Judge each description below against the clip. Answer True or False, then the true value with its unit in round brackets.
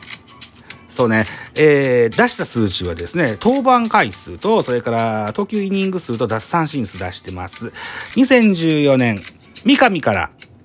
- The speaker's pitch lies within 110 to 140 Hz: True (135 Hz)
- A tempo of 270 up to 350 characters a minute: False (255 characters per minute)